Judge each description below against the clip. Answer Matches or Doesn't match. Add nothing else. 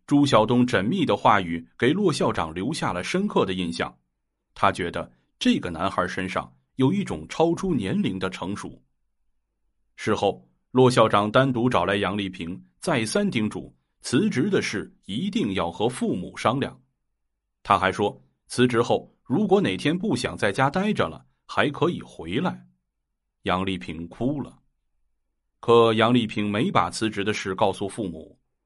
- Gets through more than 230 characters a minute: Doesn't match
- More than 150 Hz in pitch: Doesn't match